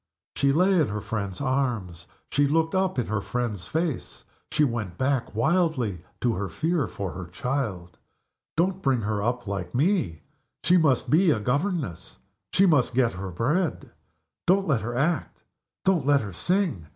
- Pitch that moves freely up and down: Yes, wide, 8.0 semitones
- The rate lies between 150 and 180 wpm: Yes, average, 165 wpm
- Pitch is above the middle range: No, low, 130 Hz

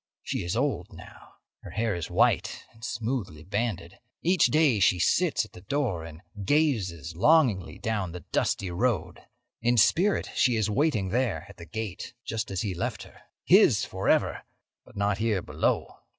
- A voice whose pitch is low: Yes, low, 105 Hz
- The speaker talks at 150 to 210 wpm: Yes, average, 165 wpm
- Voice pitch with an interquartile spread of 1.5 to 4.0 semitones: No, average, 5.3 semitones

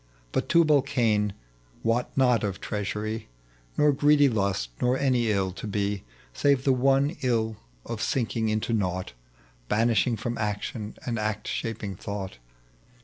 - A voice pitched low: Yes, low, 110 Hz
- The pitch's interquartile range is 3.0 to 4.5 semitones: Yes, average, 3.7 semitones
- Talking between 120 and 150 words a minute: Yes, slow, 135 wpm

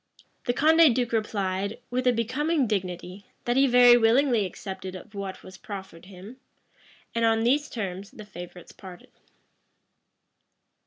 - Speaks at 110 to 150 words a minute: Yes, average, 140 wpm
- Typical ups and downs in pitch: Yes, average, 4.5 semitones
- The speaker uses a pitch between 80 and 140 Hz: No, high, 220 Hz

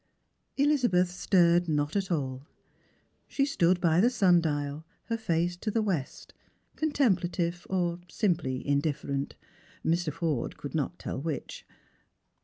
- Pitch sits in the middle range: Yes, medium, 175 Hz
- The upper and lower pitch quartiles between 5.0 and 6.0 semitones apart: No, average, 4.1 semitones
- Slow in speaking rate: Yes, slow, 125 wpm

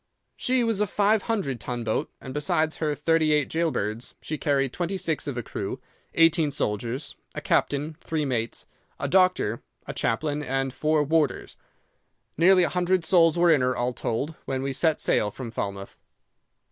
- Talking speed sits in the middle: Yes, average, 175 wpm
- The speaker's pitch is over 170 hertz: No, medium, 150 Hz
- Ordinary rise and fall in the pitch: Yes, average, 4.7 semitones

